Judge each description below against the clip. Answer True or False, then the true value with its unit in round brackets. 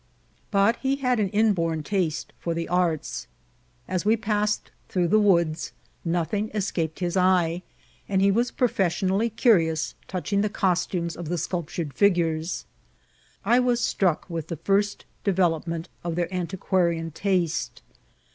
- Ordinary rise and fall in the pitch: True (3.5 semitones)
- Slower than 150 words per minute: True (140 wpm)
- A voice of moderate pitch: True (180 Hz)